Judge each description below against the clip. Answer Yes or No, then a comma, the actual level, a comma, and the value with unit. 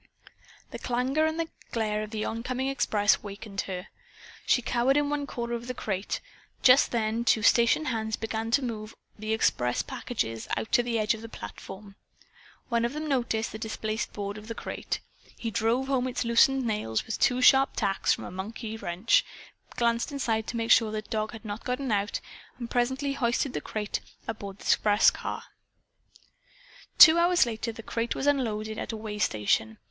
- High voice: Yes, high, 225 Hz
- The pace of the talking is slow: No, average, 180 wpm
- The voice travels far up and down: No, average, 2.8 semitones